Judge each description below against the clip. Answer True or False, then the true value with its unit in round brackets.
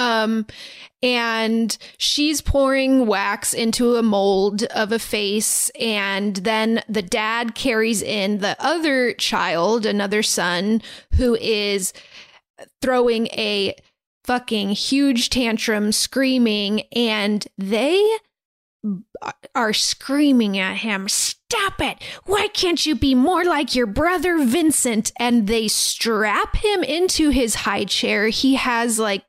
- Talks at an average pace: False (120 wpm)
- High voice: True (230 Hz)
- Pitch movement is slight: False (3.9 semitones)